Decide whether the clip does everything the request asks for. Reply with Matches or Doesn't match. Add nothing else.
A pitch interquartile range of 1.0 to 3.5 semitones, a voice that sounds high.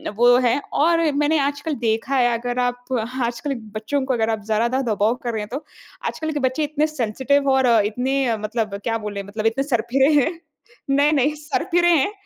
Doesn't match